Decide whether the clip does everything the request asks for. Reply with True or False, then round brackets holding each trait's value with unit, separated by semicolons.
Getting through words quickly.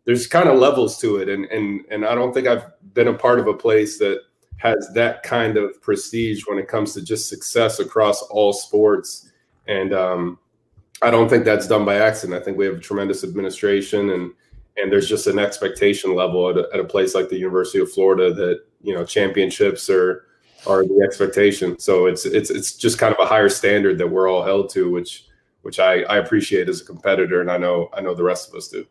True (225 wpm)